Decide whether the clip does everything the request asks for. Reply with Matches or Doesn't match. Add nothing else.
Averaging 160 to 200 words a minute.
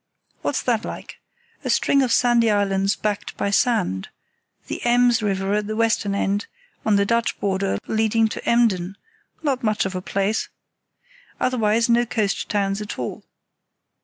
Doesn't match